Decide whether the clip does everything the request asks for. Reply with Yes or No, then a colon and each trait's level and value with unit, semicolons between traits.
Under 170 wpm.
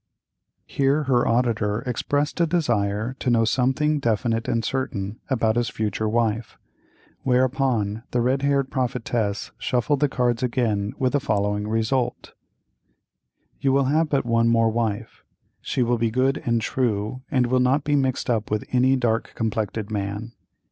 Yes: average, 155 wpm